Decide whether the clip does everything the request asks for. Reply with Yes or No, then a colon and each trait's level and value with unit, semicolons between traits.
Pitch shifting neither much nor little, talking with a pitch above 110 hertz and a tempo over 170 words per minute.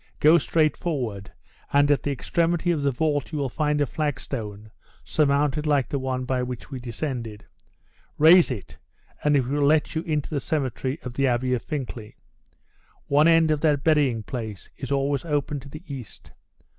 Yes: average, 3.1 semitones; medium, 140 Hz; average, 180 wpm